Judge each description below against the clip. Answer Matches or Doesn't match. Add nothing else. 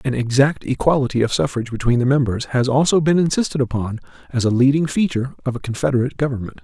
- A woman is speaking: Doesn't match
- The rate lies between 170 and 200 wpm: Matches